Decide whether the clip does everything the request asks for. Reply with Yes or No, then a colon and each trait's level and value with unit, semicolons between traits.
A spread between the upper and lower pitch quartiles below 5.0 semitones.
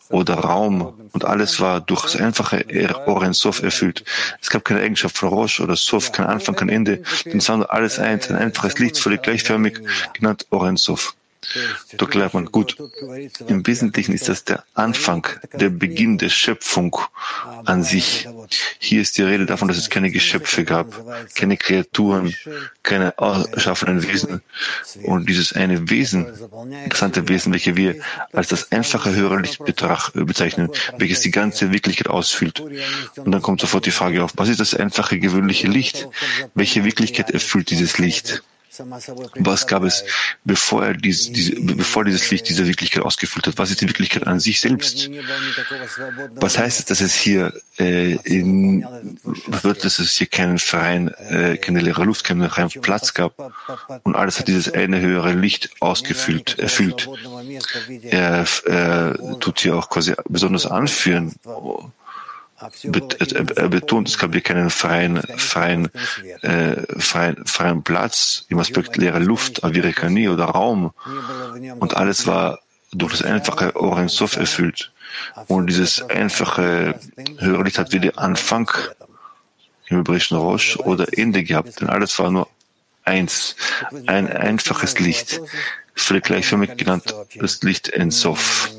Yes: average, 3.7 semitones